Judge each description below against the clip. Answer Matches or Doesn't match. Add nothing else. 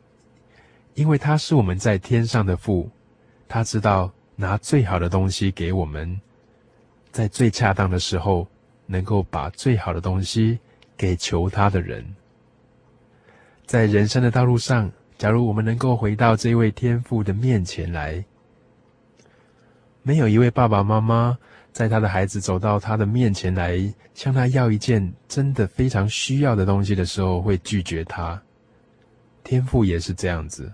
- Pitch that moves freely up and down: Doesn't match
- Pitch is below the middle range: Matches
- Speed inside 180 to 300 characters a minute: Matches